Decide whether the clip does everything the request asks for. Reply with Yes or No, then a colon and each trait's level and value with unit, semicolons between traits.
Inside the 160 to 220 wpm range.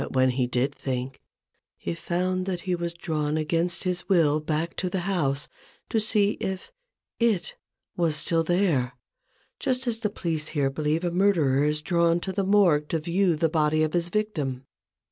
Yes: average, 180 wpm